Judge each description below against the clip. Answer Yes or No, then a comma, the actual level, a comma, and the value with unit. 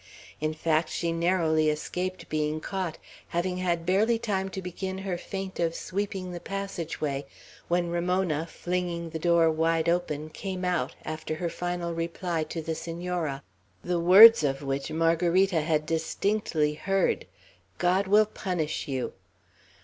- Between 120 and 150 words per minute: Yes, average, 145 wpm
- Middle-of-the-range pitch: Yes, medium, 170 Hz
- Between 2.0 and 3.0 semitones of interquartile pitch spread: Yes, average, 2.7 semitones